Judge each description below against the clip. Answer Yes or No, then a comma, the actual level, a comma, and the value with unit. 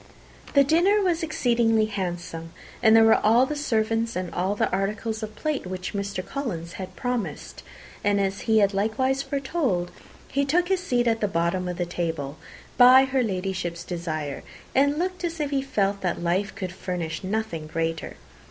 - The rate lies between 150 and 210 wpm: Yes, average, 175 wpm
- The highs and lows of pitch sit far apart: Yes, wide, 6.6 semitones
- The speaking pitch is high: Yes, high, 210 Hz